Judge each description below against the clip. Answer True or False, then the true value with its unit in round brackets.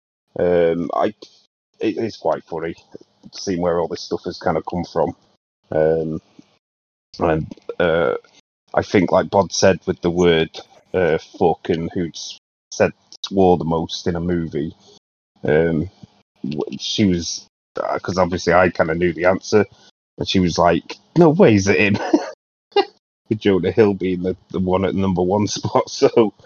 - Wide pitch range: False (2.6 semitones)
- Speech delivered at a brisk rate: False (165 wpm)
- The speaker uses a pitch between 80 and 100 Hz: True (90 Hz)